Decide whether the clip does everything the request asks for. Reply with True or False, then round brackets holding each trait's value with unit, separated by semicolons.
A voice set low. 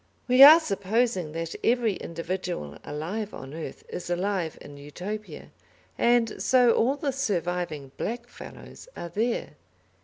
False (195 Hz)